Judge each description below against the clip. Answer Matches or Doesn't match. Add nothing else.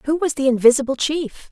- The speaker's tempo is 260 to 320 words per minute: Doesn't match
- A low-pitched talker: Doesn't match